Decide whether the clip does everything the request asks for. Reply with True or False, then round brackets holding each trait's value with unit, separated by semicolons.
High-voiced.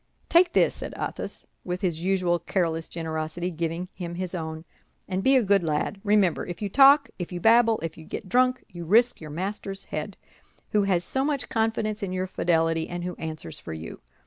False (180 Hz)